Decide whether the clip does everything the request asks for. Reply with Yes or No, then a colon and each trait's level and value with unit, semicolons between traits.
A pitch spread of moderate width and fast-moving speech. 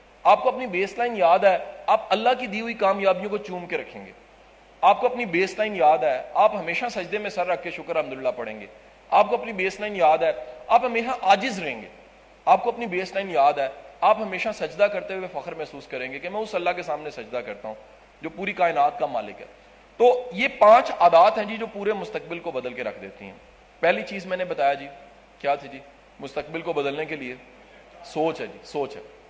No: wide, 6.1 semitones; fast, 235 wpm